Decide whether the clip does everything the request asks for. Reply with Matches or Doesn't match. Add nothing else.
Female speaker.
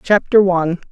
Matches